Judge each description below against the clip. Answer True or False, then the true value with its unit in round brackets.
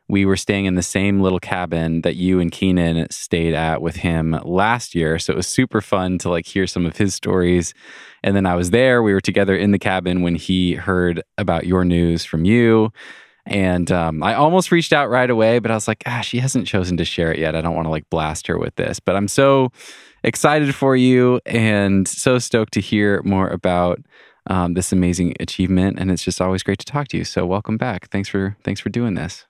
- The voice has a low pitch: True (95 Hz)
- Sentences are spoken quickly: True (230 wpm)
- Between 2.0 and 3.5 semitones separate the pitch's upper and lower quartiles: False (3.9 semitones)